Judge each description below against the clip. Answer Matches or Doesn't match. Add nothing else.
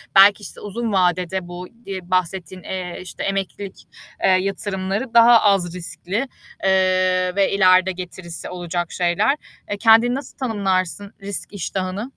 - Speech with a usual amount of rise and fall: Doesn't match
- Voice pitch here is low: Doesn't match